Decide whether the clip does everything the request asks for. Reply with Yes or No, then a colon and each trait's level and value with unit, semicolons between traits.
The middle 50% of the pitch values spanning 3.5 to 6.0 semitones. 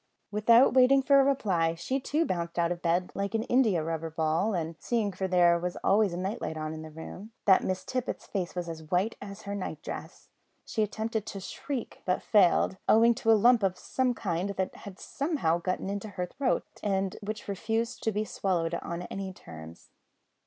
Yes: average, 4.5 semitones